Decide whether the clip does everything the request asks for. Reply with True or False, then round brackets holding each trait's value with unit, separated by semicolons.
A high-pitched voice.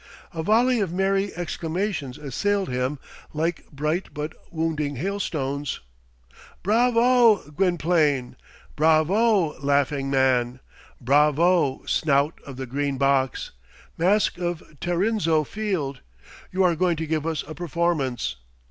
False (160 Hz)